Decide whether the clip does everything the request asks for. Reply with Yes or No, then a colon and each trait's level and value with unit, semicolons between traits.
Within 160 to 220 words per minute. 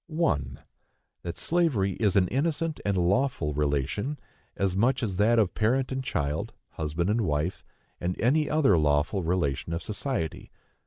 No: average, 150 wpm